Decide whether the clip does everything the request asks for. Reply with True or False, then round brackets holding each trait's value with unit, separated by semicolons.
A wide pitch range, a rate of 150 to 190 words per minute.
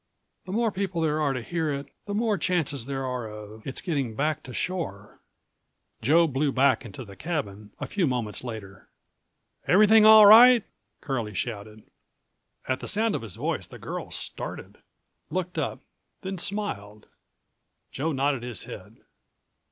True (8.4 semitones; 155 wpm)